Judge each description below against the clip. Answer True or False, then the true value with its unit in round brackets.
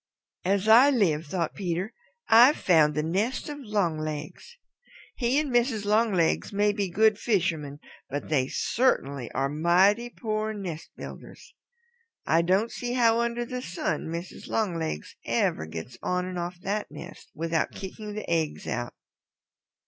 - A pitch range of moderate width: False (5.7 semitones)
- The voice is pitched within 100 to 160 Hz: False (190 Hz)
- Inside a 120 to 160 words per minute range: True (145 wpm)